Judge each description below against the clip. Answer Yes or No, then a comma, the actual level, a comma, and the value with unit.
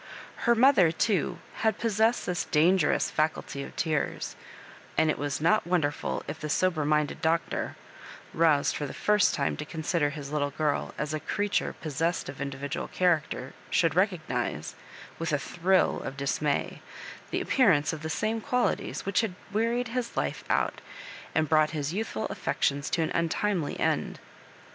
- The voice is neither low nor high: Yes, medium, 160 Hz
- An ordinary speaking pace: Yes, average, 165 wpm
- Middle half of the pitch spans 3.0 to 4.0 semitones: No, average, 4.6 semitones